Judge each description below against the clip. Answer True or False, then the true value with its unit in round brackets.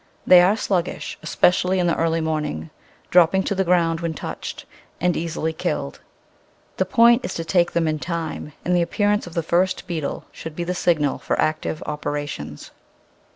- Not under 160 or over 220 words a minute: True (175 wpm)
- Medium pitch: True (170 Hz)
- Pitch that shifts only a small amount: True (2.2 semitones)